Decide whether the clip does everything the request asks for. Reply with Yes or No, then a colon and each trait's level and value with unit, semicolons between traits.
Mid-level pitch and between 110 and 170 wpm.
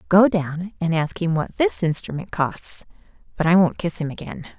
No: medium, 175 Hz; average, 195 wpm